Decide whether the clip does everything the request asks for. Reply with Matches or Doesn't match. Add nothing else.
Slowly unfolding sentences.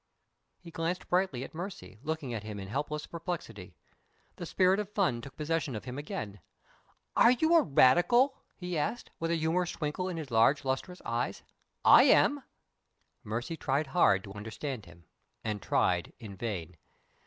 Doesn't match